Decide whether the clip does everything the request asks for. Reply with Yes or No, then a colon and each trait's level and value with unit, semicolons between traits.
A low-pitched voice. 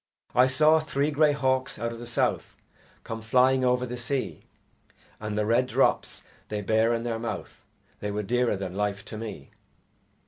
Yes: low, 120 Hz